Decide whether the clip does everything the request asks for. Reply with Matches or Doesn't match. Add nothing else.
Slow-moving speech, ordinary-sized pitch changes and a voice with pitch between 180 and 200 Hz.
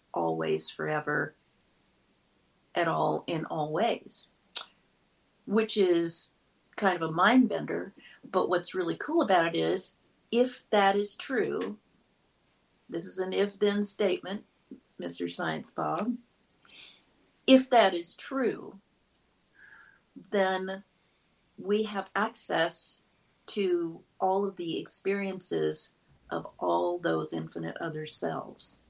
Matches